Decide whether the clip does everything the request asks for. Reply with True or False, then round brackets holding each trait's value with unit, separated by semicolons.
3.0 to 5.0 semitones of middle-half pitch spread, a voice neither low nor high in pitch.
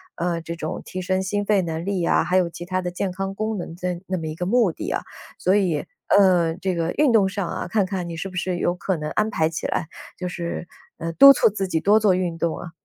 False (2.4 semitones; 180 Hz)